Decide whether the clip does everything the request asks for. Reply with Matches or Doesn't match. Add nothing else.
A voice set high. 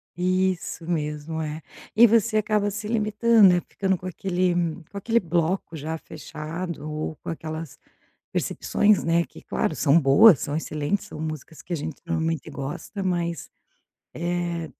Doesn't match